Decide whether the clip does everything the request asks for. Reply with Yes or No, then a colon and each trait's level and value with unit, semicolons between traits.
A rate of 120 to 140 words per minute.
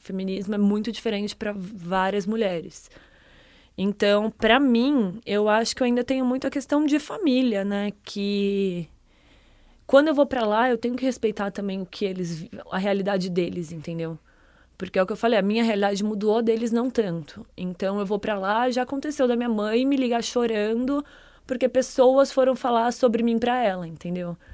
No: fast, 185 wpm